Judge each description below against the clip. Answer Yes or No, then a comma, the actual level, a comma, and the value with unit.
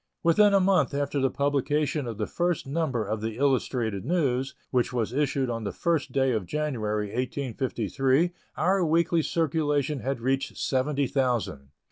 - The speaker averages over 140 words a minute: Yes, average, 155 wpm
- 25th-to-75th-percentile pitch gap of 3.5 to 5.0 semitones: Yes, average, 4.0 semitones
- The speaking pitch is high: No, low, 135 Hz